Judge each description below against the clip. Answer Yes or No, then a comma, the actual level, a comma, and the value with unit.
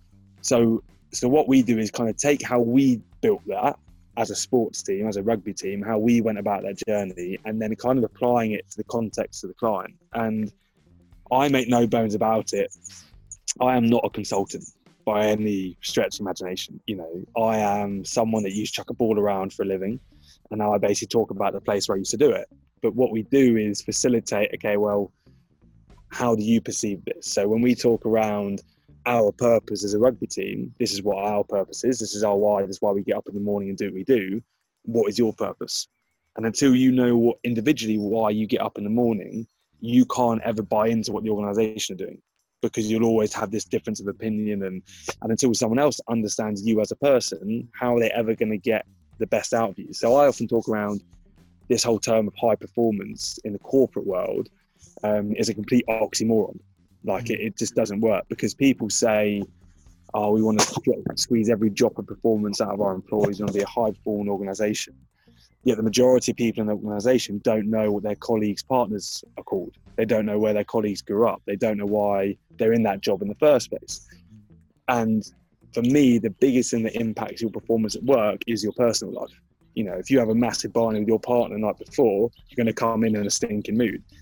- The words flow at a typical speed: No, fast, 225 wpm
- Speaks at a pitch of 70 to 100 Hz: No, low, 110 Hz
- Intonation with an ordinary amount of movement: No, narrow, 2.3 semitones